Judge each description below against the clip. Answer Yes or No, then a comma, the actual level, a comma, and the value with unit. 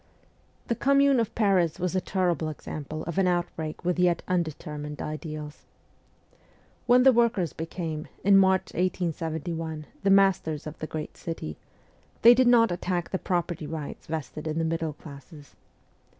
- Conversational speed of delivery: Yes, average, 150 wpm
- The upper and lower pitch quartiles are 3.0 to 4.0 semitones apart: Yes, average, 3.4 semitones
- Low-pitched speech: No, medium, 170 Hz